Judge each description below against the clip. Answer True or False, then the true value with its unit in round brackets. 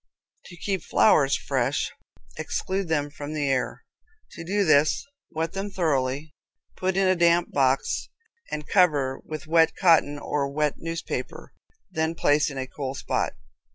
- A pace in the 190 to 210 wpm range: False (155 wpm)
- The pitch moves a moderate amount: True (3.2 semitones)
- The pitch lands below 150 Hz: False (155 Hz)